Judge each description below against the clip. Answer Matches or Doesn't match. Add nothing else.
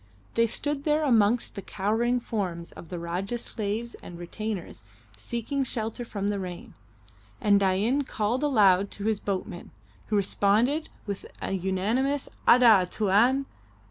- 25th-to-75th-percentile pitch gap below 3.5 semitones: Doesn't match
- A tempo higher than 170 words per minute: Doesn't match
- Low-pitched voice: Doesn't match